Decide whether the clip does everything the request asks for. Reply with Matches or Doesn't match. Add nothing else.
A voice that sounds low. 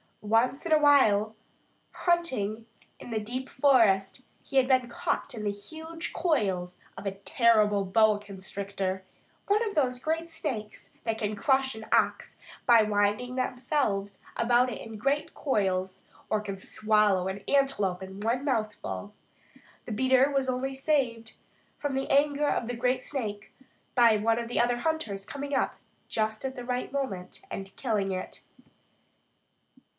Doesn't match